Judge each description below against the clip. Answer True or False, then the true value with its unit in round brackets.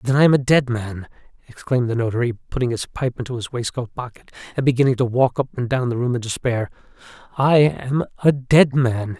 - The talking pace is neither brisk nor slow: False (210 wpm)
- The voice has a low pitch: True (125 Hz)